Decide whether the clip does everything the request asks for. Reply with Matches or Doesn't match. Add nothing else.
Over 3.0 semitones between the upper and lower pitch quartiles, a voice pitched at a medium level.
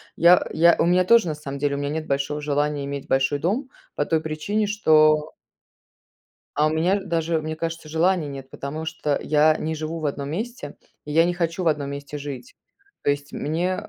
Doesn't match